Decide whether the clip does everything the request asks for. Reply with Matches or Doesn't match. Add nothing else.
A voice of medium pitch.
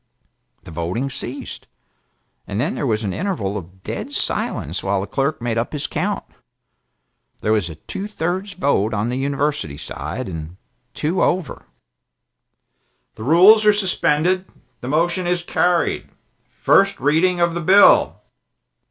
Matches